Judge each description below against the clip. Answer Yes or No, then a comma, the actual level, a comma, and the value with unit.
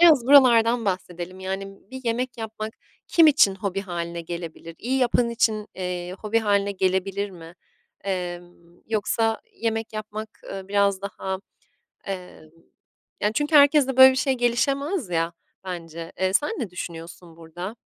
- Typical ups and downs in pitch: Yes, average, 4.7 semitones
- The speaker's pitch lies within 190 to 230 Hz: Yes, high, 200 Hz